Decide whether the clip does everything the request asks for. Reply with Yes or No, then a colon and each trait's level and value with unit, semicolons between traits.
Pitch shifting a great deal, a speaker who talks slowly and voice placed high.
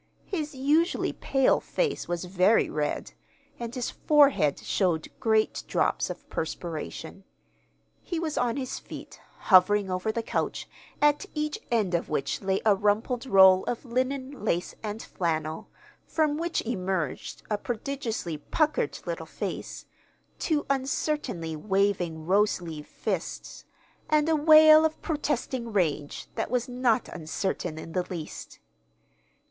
Yes: wide, 7.6 semitones; slow, 130 wpm; high, 220 Hz